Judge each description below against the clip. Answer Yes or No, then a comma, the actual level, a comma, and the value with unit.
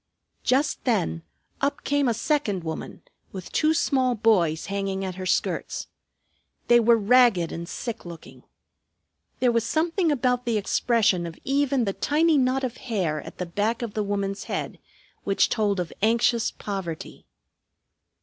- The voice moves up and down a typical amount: Yes, average, 4.9 semitones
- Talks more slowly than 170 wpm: Yes, average, 150 wpm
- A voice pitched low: No, high, 225 Hz